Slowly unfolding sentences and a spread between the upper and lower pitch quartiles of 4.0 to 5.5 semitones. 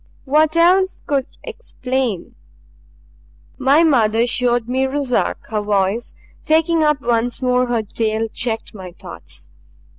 Yes: slow, 120 wpm; average, 4.6 semitones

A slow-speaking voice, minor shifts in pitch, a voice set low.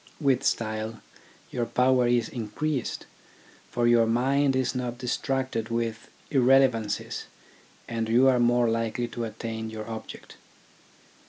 Yes: slow, 120 wpm; narrow, 2.2 semitones; low, 120 Hz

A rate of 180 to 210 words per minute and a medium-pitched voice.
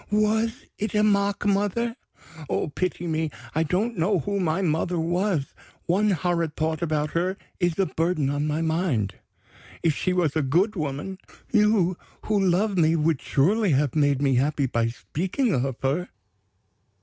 No: average, 160 wpm; medium, 170 Hz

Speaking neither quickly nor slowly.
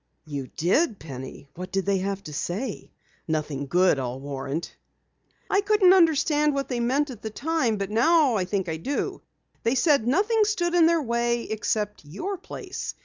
Yes: average, 180 wpm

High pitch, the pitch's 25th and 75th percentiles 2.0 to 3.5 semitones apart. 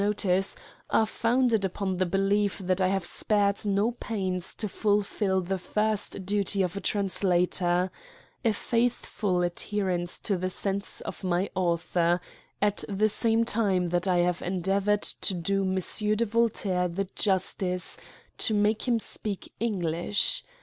Yes: high, 195 Hz; narrow, 2.4 semitones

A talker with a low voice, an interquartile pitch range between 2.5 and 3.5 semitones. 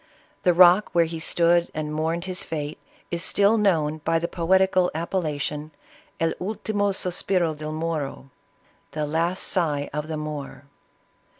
No: medium, 165 Hz; average, 3.0 semitones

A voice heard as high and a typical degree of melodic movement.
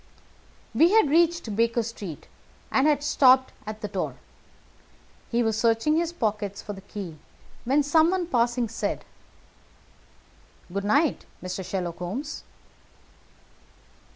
No: high, 235 Hz; wide, 6.4 semitones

